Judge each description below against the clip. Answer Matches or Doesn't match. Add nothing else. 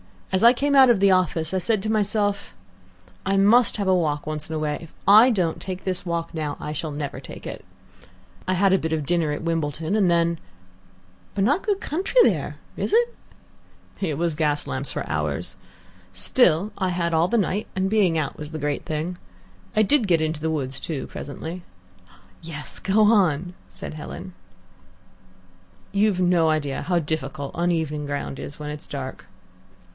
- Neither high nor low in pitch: Matches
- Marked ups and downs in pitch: Doesn't match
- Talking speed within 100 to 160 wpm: Doesn't match